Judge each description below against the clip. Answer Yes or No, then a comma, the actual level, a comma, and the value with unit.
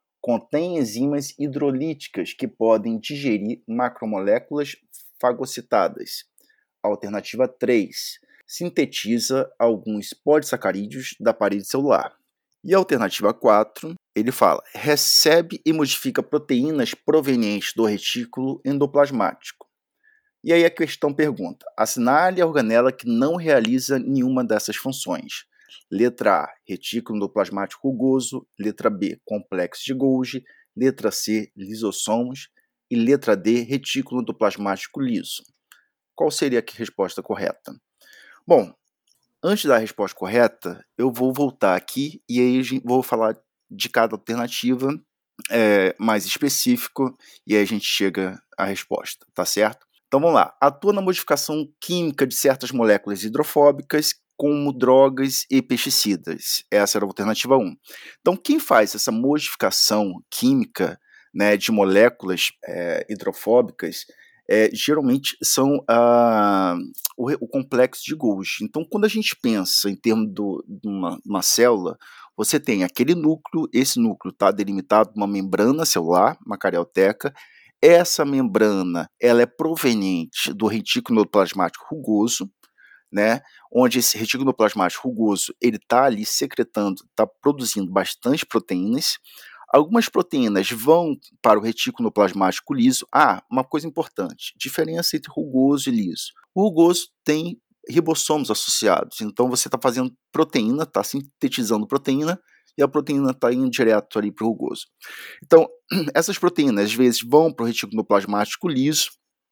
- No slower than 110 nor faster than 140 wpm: Yes, average, 125 wpm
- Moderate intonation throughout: No, wide, 5.9 semitones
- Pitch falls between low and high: No, low, 130 Hz